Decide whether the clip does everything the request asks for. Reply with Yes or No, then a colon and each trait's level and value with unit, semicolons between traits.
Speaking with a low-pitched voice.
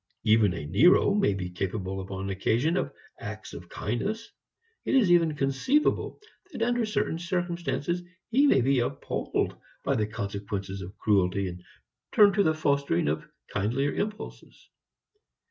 Yes: low, 125 Hz